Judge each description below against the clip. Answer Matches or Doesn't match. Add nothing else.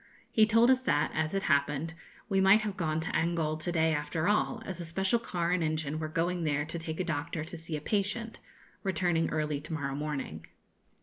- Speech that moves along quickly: Matches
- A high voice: Doesn't match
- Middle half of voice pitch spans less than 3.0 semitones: Doesn't match